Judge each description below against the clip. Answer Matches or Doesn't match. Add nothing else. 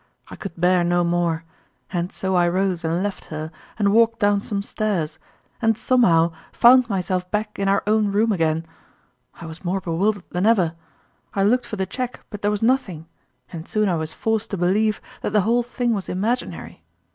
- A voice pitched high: Matches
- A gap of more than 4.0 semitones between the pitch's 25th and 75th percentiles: Doesn't match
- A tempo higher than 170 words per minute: Matches